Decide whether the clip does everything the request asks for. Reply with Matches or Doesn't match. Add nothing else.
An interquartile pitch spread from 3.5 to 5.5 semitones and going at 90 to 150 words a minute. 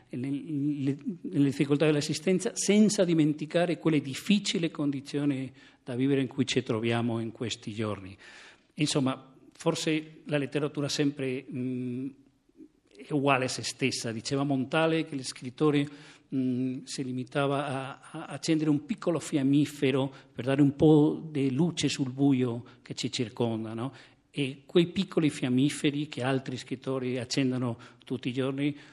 Doesn't match